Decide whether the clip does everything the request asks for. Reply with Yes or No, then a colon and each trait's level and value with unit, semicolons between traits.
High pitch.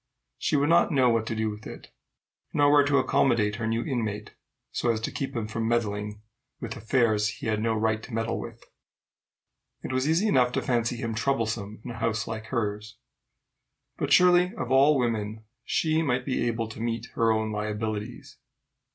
No: low, 115 Hz